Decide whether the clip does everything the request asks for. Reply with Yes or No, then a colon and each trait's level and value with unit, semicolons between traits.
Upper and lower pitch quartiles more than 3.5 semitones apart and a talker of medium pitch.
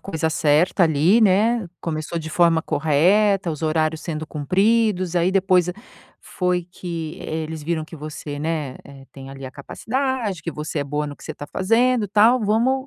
Yes: average, 4.6 semitones; medium, 170 Hz